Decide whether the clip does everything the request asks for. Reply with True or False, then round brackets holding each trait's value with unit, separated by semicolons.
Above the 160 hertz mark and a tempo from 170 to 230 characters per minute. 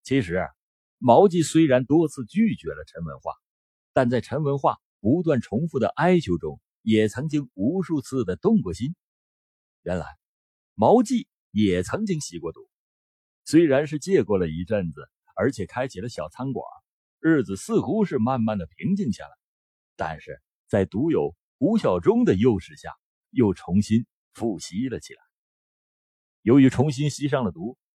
False (140 Hz; 225 characters per minute)